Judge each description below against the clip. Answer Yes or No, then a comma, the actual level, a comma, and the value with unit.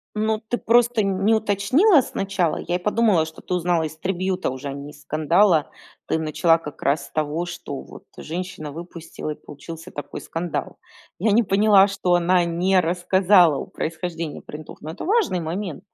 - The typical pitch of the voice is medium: Yes, medium, 175 Hz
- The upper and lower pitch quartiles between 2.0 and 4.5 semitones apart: Yes, average, 3.8 semitones